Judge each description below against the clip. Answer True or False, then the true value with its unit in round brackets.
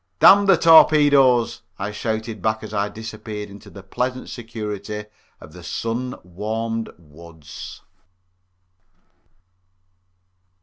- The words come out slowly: True (100 wpm)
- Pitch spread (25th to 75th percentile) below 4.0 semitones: True (3.0 semitones)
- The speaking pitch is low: True (110 Hz)